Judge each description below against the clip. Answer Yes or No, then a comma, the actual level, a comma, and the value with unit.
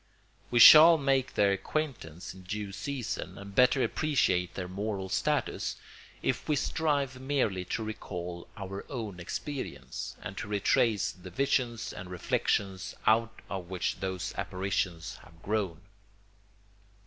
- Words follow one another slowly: Yes, slow, 130 wpm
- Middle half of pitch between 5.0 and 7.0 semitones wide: Yes, wide, 5.6 semitones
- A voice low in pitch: Yes, low, 100 Hz